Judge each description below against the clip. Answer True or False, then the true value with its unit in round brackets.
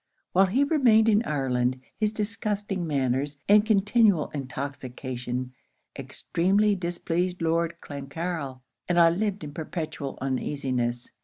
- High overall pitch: False (165 Hz)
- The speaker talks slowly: True (110 wpm)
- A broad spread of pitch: True (7.0 semitones)